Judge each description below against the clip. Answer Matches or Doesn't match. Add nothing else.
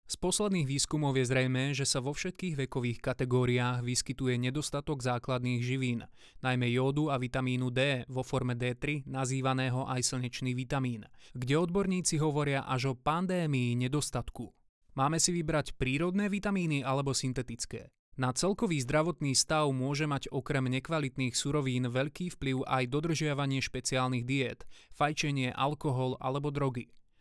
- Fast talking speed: Doesn't match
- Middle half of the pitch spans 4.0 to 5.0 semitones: Doesn't match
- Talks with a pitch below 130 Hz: Doesn't match